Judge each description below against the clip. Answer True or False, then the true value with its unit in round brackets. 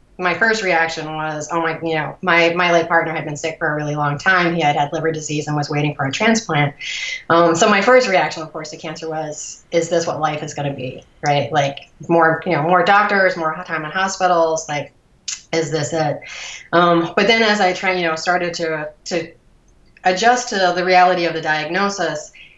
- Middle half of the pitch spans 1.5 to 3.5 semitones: True (2.8 semitones)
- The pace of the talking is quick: True (220 wpm)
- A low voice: False (165 Hz)